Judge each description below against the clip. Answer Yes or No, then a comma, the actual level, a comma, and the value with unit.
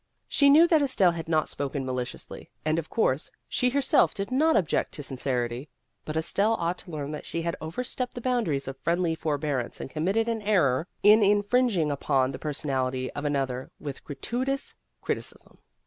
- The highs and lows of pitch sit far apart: Yes, wide, 8.0 semitones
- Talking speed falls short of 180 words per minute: No, average, 185 wpm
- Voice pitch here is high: No, medium, 160 Hz